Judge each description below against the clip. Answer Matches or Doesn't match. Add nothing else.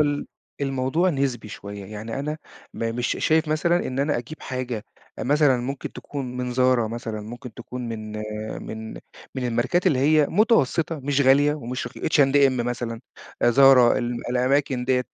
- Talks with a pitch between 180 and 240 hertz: Doesn't match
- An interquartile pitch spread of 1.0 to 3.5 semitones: Matches